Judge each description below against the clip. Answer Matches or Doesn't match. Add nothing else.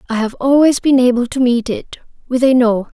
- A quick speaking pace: Matches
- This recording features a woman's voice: Matches